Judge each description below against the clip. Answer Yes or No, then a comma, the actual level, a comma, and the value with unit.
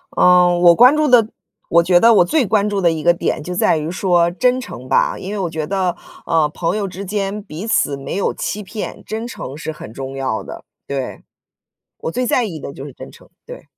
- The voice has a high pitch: No, medium, 180 Hz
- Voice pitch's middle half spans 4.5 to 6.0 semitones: Yes, average, 4.9 semitones